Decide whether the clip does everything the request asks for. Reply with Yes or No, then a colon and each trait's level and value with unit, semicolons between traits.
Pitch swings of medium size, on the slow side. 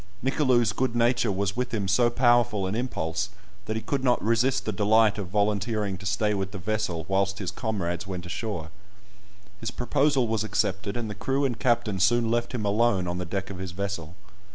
No: average, 3.6 semitones; average, 200 wpm